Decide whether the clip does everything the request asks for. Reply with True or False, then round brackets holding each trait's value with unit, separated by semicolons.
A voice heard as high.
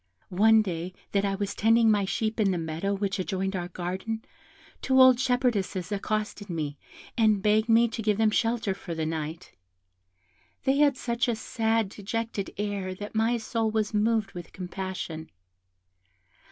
True (210 Hz)